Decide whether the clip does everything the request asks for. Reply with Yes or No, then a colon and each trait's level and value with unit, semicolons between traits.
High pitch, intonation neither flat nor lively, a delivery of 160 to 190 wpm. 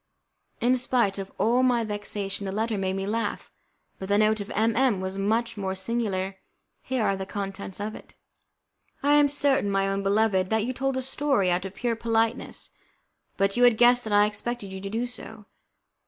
No: high, 215 Hz; average, 3.5 semitones; average, 200 wpm